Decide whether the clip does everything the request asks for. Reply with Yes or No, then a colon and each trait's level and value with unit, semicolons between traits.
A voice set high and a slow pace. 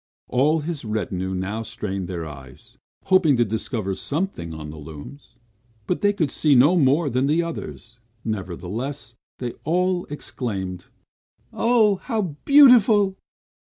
No: low, 130 Hz; slow, 130 wpm